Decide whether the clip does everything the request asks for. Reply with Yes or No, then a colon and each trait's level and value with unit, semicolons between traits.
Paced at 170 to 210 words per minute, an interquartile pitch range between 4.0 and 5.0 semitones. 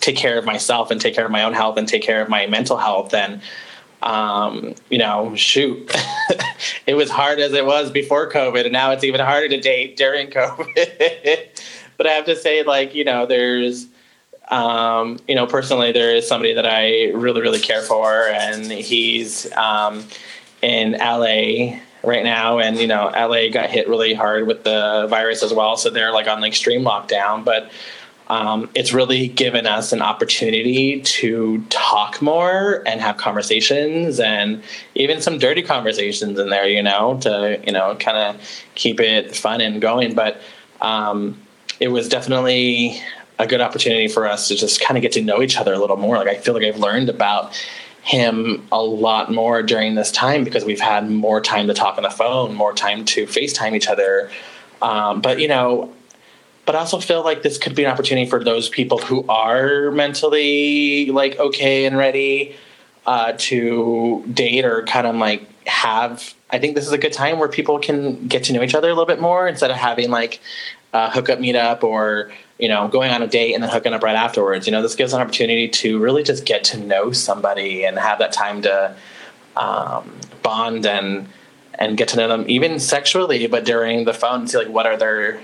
Yes: average, 200 wpm; average, 4.5 semitones